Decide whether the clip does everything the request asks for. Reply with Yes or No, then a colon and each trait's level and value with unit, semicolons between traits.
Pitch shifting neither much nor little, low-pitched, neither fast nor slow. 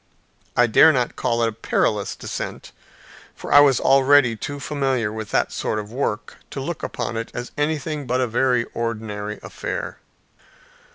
Yes: average, 3.8 semitones; low, 120 Hz; average, 165 wpm